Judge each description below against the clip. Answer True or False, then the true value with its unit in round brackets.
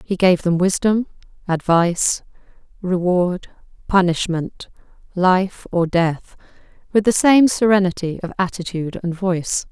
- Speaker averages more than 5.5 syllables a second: False (4.3 syllables/s)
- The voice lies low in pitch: False (185 Hz)